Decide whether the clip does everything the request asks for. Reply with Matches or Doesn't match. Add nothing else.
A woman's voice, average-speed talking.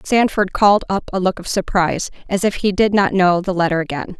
Doesn't match